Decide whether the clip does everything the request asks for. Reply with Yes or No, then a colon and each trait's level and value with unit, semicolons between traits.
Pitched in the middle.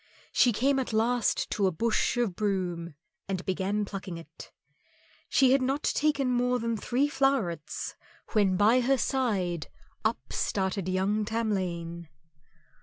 No: high, 210 Hz